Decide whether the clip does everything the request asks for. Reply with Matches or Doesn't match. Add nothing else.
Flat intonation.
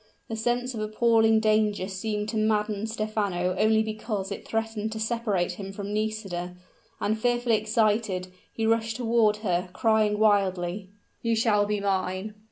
Matches